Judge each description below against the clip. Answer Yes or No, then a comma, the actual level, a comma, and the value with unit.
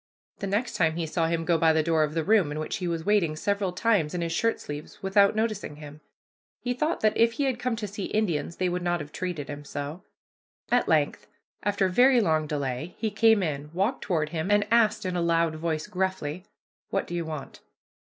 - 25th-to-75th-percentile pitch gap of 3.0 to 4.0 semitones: No, average, 4.8 semitones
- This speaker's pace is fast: Yes, fast, 225 wpm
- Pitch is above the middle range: No, medium, 175 Hz